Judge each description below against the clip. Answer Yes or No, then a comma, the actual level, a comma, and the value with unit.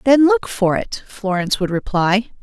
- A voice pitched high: Yes, high, 215 Hz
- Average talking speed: Yes, average, 175 wpm